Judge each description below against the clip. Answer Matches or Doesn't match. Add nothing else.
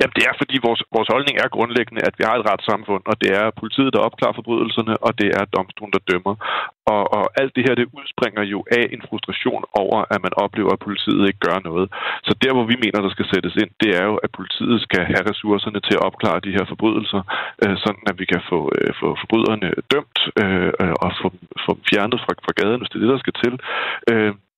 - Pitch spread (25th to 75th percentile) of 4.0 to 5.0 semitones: Doesn't match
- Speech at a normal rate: Doesn't match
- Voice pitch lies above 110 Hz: Doesn't match